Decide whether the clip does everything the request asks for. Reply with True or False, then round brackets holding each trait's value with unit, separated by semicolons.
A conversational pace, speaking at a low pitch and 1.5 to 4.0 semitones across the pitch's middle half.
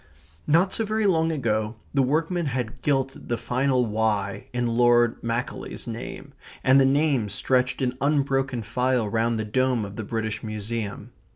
True (160 wpm; 125 Hz; 3.4 semitones)